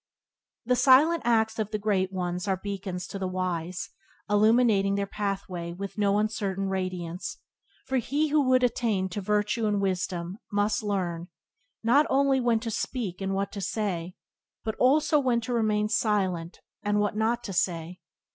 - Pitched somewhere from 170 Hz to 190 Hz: No, high, 205 Hz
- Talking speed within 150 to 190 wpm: Yes, average, 160 wpm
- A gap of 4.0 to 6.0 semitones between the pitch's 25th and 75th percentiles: No, average, 3.5 semitones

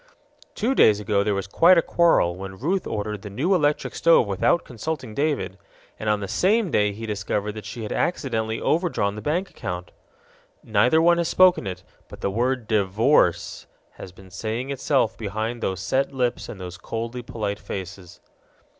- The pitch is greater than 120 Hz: No, low, 110 Hz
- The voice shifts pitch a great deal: Yes, wide, 6.0 semitones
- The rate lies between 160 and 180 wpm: Yes, average, 175 wpm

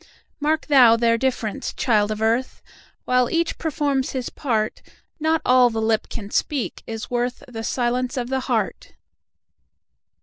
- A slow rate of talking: Yes, slow, 130 wpm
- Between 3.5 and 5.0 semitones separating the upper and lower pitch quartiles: No, average, 3.0 semitones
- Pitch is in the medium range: No, high, 245 Hz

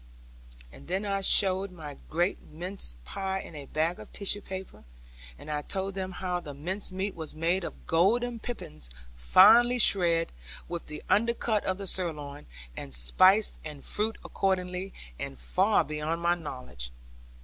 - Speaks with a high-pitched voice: No, medium, 180 Hz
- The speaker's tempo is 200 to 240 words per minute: No, average, 155 wpm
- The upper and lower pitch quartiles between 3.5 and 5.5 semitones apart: Yes, average, 4.3 semitones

